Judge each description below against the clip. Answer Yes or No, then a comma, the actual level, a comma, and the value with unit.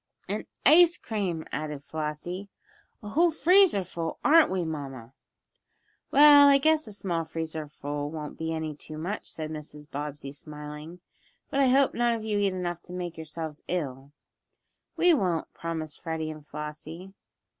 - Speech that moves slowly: No, average, 155 wpm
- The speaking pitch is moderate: Yes, medium, 165 Hz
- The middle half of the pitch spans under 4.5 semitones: No, wide, 5.4 semitones